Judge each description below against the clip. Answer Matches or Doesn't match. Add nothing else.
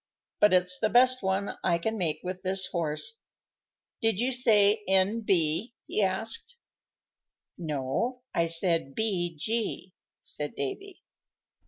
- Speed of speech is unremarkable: Doesn't match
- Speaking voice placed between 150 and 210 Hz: Matches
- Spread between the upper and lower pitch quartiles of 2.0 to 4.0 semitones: Doesn't match